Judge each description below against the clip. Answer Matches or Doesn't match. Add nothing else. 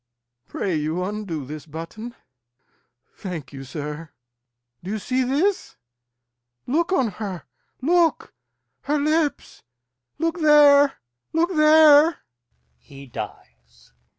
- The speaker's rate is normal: Doesn't match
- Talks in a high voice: Matches